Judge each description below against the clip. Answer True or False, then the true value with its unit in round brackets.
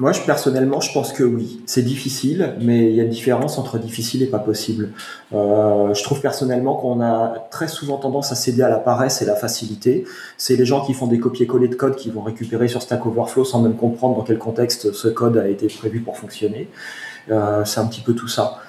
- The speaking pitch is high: False (120 Hz)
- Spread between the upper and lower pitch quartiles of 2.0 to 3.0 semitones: True (2.5 semitones)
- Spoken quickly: True (230 wpm)